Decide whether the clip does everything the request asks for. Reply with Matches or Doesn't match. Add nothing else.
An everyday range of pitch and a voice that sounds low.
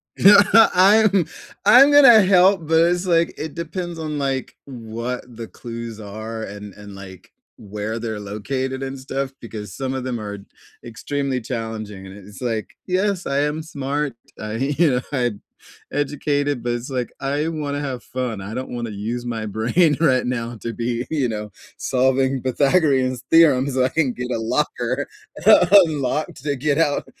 Matches